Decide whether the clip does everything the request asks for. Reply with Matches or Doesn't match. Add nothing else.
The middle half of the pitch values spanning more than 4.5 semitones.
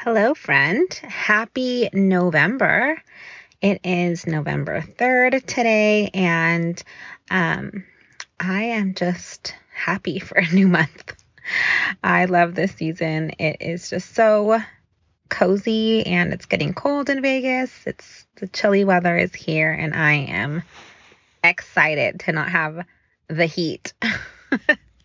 Matches